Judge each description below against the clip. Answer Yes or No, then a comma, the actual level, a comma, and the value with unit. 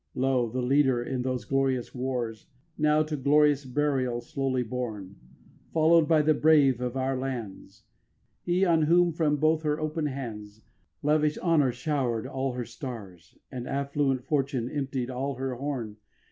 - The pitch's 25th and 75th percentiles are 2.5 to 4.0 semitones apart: Yes, average, 3.3 semitones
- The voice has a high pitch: No, low, 135 Hz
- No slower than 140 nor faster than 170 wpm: Yes, average, 155 wpm